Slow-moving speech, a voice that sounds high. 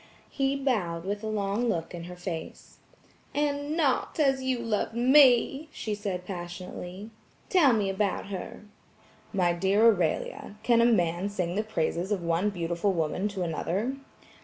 No: average, 155 wpm; high, 200 Hz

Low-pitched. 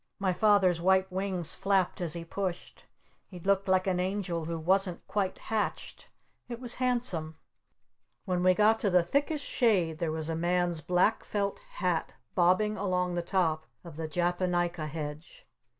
No: medium, 180 Hz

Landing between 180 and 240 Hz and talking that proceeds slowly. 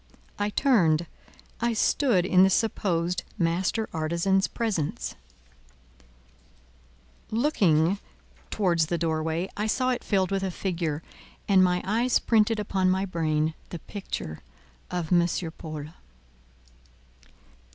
Yes: medium, 185 Hz; slow, 115 wpm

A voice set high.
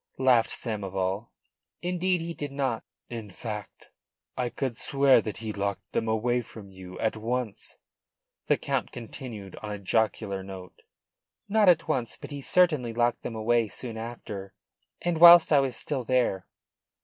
No: low, 115 Hz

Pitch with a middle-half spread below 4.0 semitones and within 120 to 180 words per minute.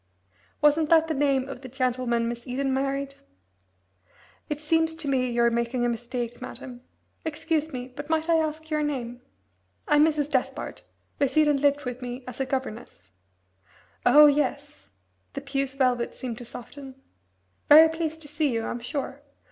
Yes: average, 3.3 semitones; average, 160 wpm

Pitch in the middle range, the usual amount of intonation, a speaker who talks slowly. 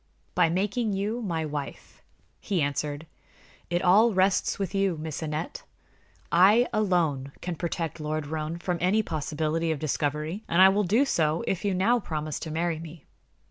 No: medium, 170 Hz; average, 3.9 semitones; average, 165 wpm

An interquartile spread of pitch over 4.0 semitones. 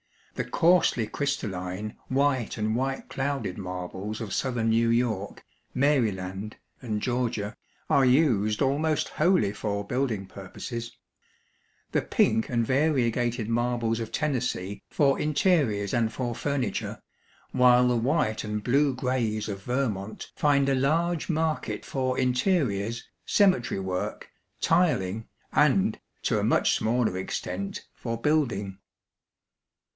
Yes: average, 4.5 semitones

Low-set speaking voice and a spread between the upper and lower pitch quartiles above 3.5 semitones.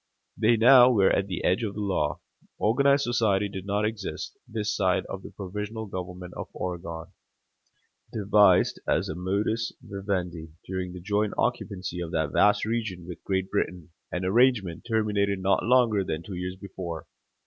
No: low, 100 Hz; average, 3.0 semitones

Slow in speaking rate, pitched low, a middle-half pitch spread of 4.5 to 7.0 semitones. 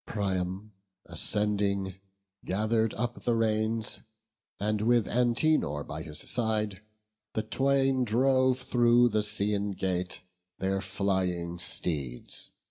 No: slow, 105 wpm; low, 105 Hz; average, 3.8 semitones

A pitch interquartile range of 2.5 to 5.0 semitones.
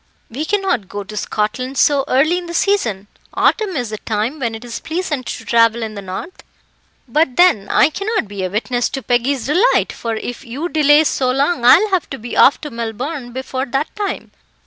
No: wide, 5.4 semitones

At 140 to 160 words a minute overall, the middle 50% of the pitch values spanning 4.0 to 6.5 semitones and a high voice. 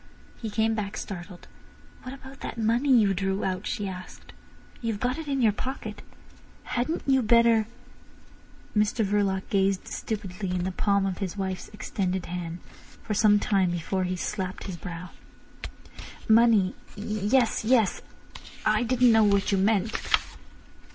No: average, 145 wpm; average, 3.2 semitones; high, 205 Hz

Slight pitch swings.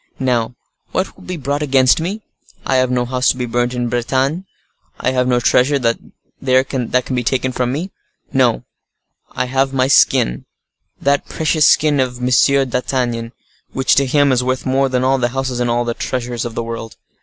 Yes: narrow, 1.8 semitones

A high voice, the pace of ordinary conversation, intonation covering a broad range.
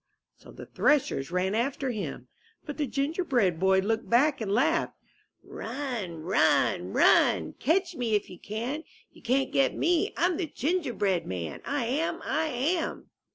Yes: very high, 255 Hz; average, 155 wpm; wide, 7.0 semitones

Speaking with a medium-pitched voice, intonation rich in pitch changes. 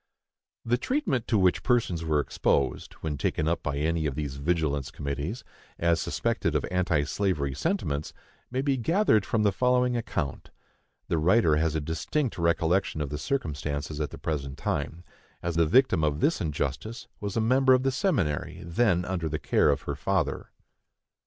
No: very low, 85 Hz; wide, 7.7 semitones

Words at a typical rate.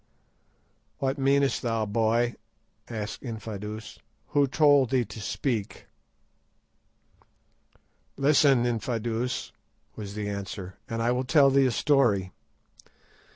No: slow, 105 wpm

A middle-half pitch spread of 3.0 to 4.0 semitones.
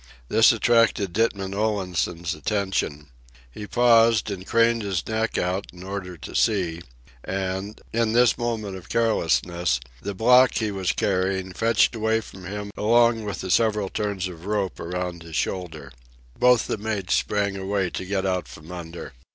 Yes: average, 3.4 semitones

